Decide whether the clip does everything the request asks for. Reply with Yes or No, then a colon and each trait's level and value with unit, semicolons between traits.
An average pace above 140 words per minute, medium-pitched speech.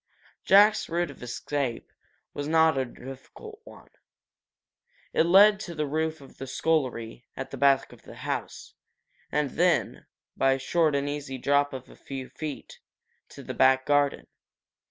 Yes: average, 155 wpm; medium, 145 Hz